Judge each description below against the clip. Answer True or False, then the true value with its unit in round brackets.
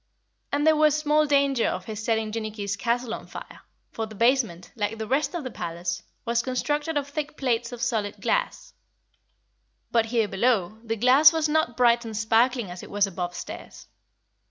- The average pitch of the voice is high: True (235 Hz)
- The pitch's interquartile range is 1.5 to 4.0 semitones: False (4.6 semitones)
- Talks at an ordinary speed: True (180 wpm)